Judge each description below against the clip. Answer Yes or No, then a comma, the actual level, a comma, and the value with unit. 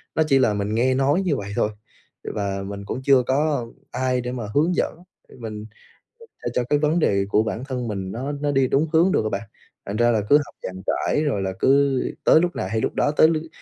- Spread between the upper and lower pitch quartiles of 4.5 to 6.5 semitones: Yes, wide, 5.6 semitones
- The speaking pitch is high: No, low, 130 Hz